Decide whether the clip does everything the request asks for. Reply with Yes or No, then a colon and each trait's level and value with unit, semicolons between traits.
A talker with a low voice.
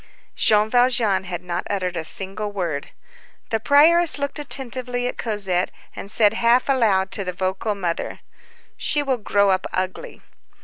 No: high, 210 Hz